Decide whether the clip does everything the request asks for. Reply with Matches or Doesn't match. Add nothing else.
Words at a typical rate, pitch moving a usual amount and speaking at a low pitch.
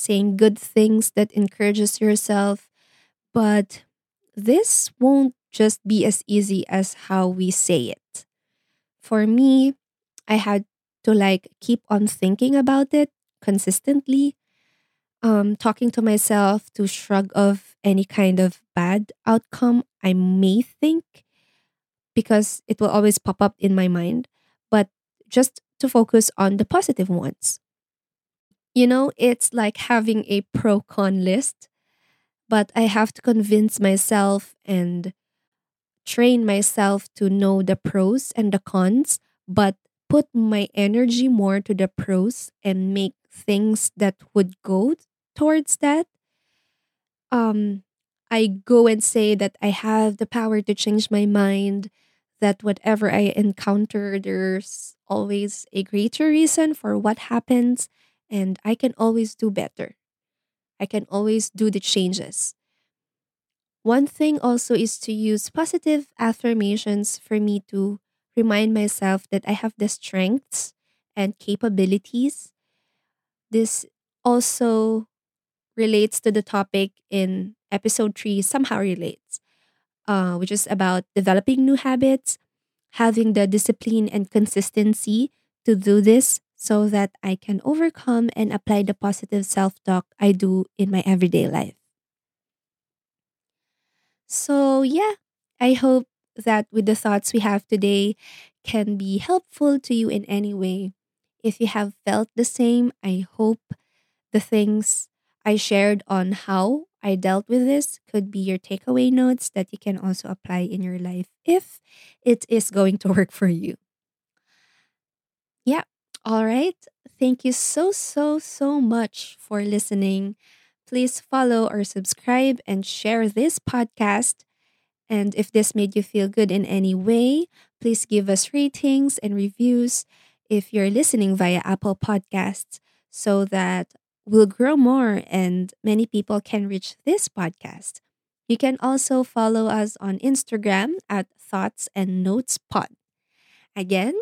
Doesn't match